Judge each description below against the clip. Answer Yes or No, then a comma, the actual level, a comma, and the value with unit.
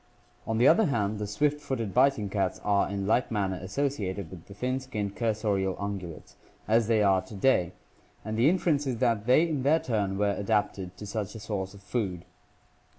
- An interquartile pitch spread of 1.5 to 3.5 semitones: No, average, 4.2 semitones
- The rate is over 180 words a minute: Yes, average, 190 wpm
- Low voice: Yes, low, 105 Hz